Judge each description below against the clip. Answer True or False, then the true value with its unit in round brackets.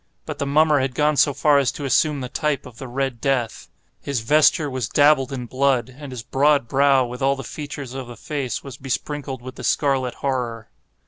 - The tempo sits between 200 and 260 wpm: True (205 wpm)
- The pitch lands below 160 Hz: True (135 Hz)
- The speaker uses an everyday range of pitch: False (2.2 semitones)